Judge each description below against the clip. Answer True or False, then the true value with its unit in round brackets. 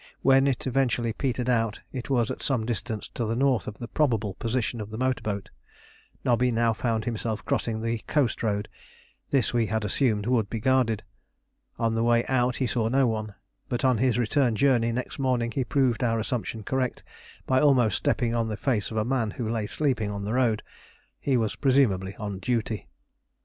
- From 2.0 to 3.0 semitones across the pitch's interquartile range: True (2.7 semitones)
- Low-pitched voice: True (115 Hz)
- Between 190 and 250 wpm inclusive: True (195 wpm)